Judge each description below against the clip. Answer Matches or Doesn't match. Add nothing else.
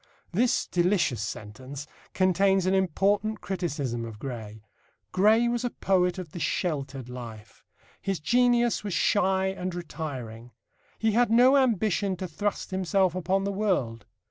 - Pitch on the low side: Doesn't match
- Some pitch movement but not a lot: Doesn't match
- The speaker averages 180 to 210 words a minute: Doesn't match